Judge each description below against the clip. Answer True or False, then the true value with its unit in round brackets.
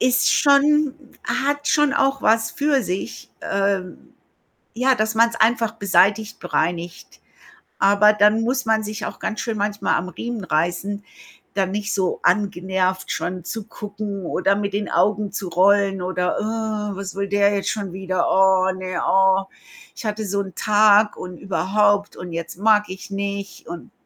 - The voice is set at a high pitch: True (200 Hz)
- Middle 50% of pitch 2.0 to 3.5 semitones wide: True (2.5 semitones)